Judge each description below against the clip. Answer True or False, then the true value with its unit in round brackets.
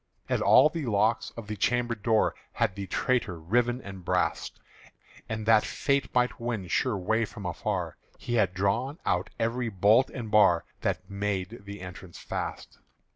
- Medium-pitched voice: False (105 Hz)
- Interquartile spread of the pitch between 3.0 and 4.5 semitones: True (3.7 semitones)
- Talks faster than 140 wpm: True (165 wpm)